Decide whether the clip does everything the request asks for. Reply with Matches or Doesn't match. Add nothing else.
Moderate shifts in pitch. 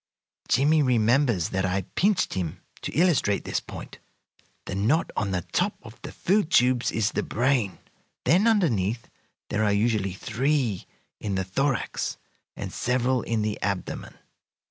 Doesn't match